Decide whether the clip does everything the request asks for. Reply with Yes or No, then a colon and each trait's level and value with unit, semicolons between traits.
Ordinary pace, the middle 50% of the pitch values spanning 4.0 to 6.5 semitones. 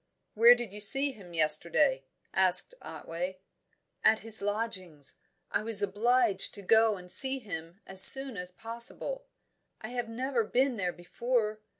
Yes: average, 150 wpm; average, 4.5 semitones